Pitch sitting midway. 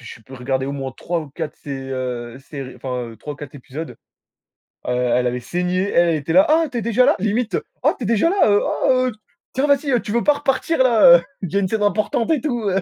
Yes: medium, 175 Hz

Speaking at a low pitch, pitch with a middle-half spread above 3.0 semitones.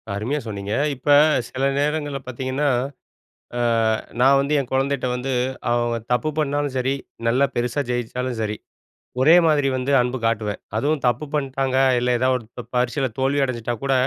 No: low, 130 Hz; narrow, 2.4 semitones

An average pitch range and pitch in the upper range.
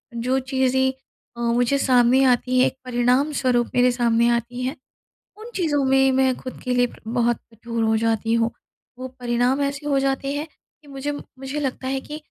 No: narrow, 2.0 semitones; very high, 260 Hz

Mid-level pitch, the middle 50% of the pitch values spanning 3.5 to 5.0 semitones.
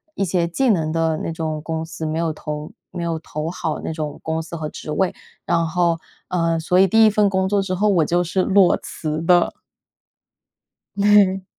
No: medium, 170 Hz; average, 2.8 semitones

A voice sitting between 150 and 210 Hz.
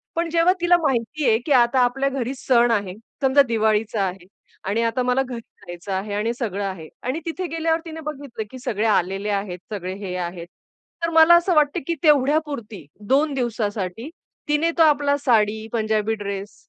No: high, 235 Hz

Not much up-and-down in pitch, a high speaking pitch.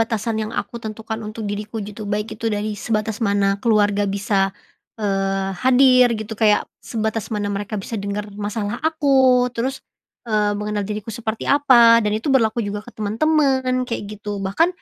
Yes: narrow, 2.1 semitones; high, 215 Hz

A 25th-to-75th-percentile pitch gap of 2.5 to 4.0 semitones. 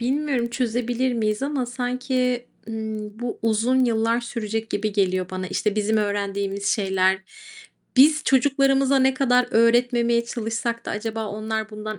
Yes: average, 2.8 semitones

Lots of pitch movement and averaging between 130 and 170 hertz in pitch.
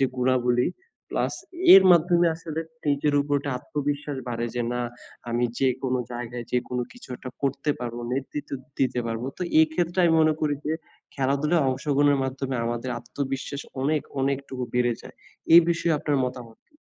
No: average, 3.1 semitones; low, 135 Hz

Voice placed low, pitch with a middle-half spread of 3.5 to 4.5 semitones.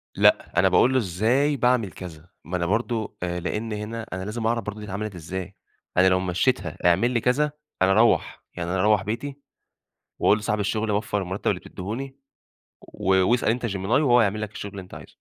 Yes: low, 105 Hz; average, 3.9 semitones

